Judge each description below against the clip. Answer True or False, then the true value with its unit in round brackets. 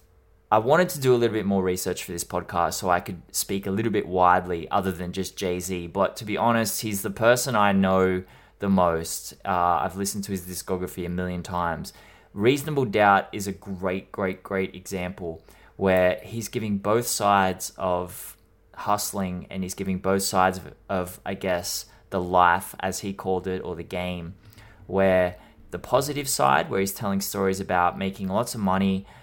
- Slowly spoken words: False (185 wpm)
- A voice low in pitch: True (95 Hz)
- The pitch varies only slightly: True (2.1 semitones)